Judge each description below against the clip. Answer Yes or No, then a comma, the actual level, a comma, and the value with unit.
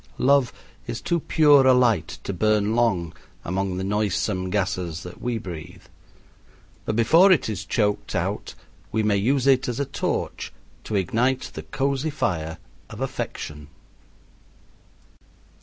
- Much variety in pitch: Yes, wide, 5.9 semitones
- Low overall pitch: Yes, low, 110 Hz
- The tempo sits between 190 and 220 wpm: No, average, 140 wpm